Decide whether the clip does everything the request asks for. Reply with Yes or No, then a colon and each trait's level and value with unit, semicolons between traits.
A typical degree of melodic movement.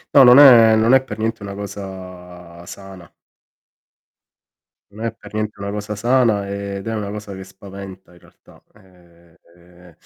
Yes: average, 3.1 semitones